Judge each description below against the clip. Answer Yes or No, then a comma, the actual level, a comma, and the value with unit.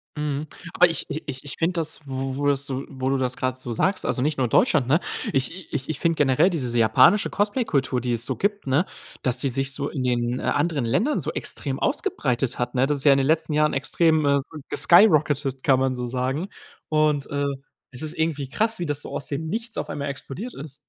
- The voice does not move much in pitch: No, average, 3.3 semitones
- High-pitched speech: No, medium, 140 Hz